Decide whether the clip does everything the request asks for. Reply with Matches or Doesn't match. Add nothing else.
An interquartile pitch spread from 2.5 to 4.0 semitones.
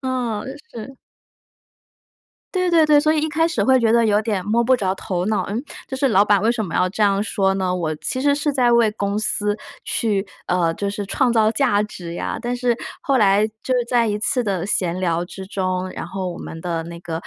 Doesn't match